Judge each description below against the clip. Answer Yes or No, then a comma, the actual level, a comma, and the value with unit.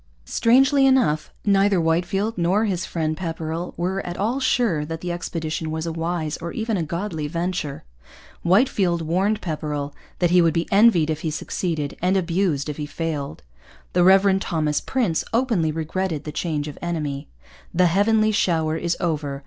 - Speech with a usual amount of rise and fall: Yes, average, 3.7 semitones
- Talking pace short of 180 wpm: Yes, average, 165 wpm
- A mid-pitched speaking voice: Yes, medium, 170 Hz